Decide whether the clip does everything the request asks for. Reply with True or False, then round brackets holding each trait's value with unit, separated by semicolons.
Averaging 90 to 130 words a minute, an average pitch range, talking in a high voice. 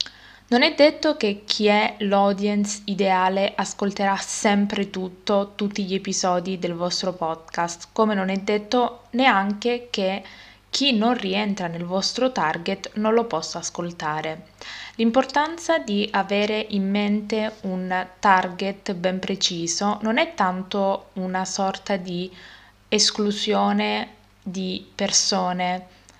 False (115 wpm; 2.3 semitones; 200 Hz)